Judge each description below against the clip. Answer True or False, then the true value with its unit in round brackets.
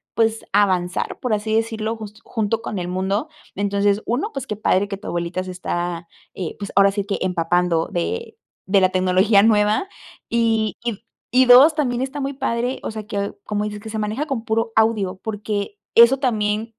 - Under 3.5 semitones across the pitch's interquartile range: True (2.8 semitones)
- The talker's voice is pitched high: True (210 Hz)